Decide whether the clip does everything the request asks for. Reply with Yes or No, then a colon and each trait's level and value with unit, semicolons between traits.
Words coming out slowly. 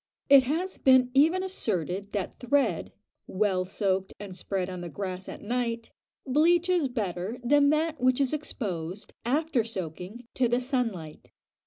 No: average, 150 wpm